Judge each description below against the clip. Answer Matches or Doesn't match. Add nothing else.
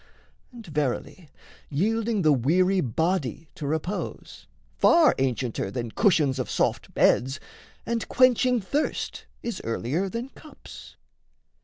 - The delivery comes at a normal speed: Doesn't match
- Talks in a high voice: Doesn't match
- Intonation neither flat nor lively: Doesn't match